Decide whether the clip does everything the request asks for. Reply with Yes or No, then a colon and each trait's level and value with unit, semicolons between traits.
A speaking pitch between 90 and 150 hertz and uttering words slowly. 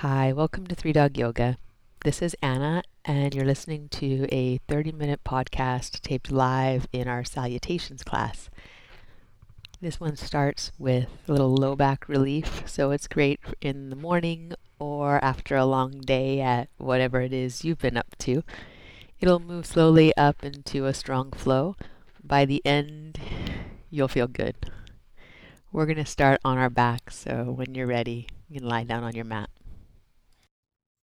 No: low, 135 Hz; average, 160 wpm